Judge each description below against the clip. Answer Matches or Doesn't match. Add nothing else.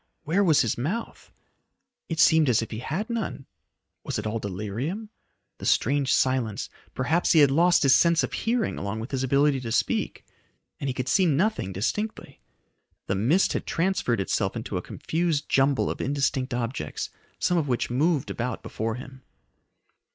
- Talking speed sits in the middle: Matches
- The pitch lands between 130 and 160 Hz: Matches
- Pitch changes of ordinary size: Doesn't match